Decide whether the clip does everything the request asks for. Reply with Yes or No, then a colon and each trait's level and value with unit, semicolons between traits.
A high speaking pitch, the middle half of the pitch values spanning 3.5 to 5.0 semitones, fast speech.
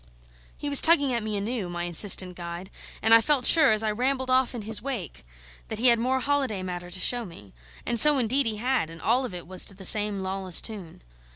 No: high, 220 Hz; wide, 5.6 semitones; fast, 230 wpm